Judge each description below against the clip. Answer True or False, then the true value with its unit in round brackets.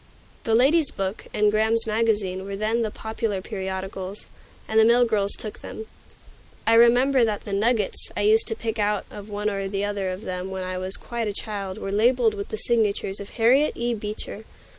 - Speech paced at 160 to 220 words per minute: True (200 wpm)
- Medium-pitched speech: False (210 Hz)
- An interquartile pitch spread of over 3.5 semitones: False (2.5 semitones)